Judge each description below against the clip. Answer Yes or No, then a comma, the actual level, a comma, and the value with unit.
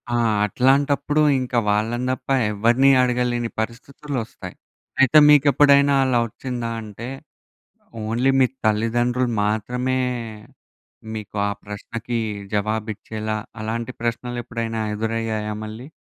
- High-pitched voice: No, low, 120 Hz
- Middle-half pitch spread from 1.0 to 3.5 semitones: Yes, narrow, 2.6 semitones